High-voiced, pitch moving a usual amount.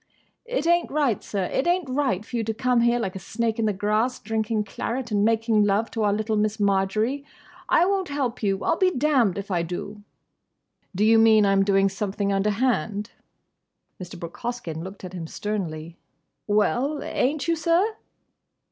Yes: high, 215 Hz; average, 4.2 semitones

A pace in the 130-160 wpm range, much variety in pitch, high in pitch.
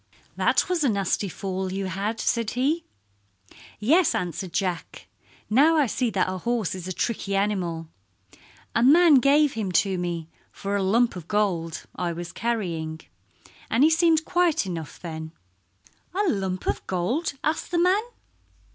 Yes: average, 155 wpm; wide, 7.4 semitones; high, 205 Hz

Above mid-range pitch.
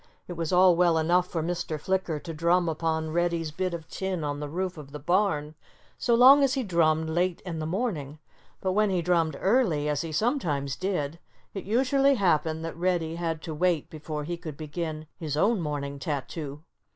No: medium, 165 Hz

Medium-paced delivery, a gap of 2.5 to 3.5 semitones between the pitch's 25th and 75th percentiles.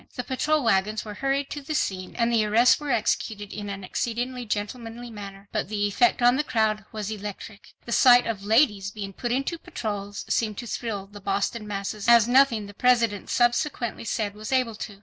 Yes: average, 195 wpm; average, 3.0 semitones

